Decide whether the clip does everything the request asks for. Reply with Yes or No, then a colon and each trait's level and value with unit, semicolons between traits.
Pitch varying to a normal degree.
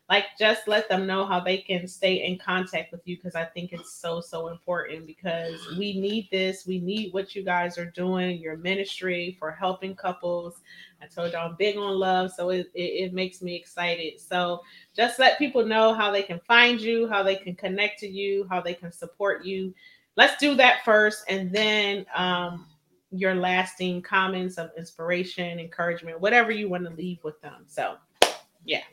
No: narrow, 2.3 semitones